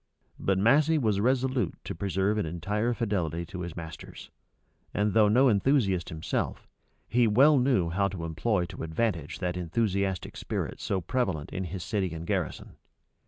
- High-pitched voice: No, low, 100 Hz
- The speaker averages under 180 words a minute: Yes, average, 160 wpm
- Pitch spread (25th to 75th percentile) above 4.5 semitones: Yes, average, 5.1 semitones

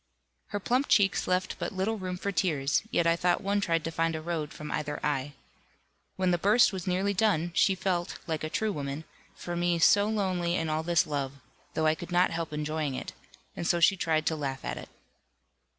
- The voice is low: No, medium, 170 Hz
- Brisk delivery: Yes, fast, 215 wpm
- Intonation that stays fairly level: No, average, 3.3 semitones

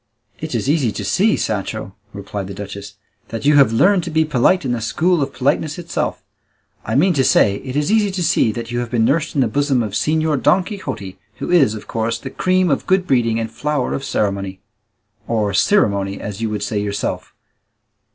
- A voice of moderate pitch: No, low, 125 Hz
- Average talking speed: No, fast, 210 wpm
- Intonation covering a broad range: Yes, wide, 6.9 semitones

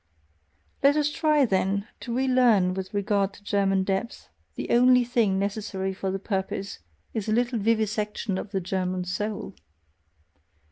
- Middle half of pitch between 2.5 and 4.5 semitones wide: Yes, average, 3.5 semitones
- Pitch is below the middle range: No, high, 205 Hz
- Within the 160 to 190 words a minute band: No, average, 145 wpm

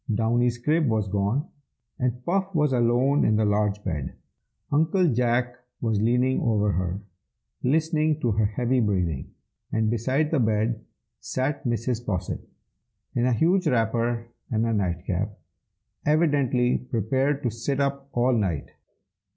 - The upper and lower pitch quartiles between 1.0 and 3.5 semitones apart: No, average, 4.1 semitones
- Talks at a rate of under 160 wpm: Yes, average, 140 wpm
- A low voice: Yes, low, 120 Hz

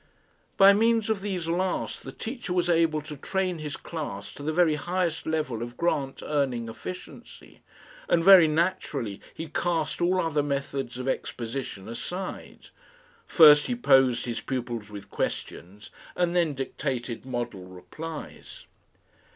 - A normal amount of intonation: No, wide, 6.1 semitones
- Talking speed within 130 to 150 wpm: Yes, average, 140 wpm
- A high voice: No, medium, 150 Hz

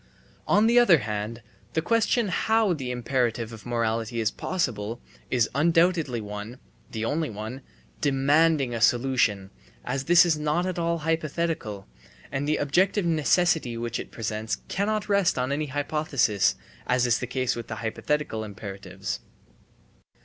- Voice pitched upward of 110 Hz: Yes, low, 135 Hz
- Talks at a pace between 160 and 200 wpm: No, average, 145 wpm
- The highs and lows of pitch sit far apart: Yes, wide, 6.5 semitones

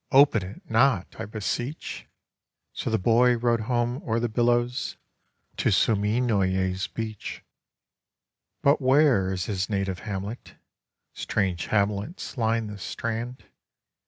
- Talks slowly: Yes, slow, 115 wpm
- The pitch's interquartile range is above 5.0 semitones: No, average, 3.4 semitones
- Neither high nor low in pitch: No, low, 110 Hz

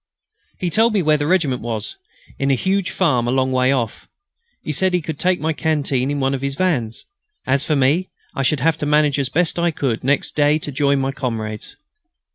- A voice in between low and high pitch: Yes, medium, 145 Hz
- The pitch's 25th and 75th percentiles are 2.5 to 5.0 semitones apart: Yes, average, 3.5 semitones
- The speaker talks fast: Yes, fast, 220 wpm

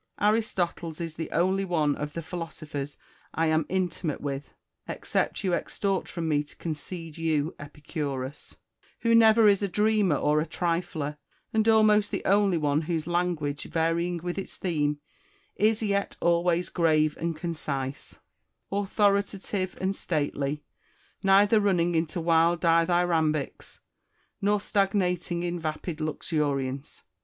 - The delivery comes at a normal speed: No, slow, 130 wpm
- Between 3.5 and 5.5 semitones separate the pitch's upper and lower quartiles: Yes, average, 4.0 semitones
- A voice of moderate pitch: Yes, medium, 170 Hz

